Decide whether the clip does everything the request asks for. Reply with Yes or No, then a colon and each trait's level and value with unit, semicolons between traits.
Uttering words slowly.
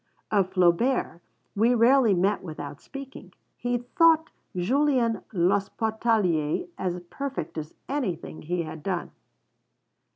Yes: slow, 105 wpm